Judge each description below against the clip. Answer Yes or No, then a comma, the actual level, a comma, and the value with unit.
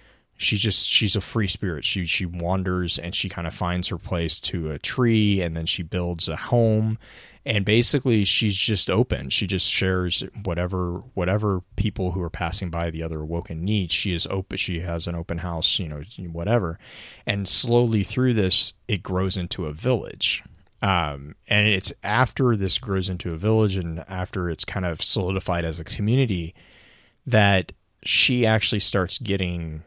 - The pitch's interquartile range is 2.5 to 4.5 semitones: Yes, average, 3.5 semitones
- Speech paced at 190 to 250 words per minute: No, average, 175 wpm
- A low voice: Yes, very low, 95 Hz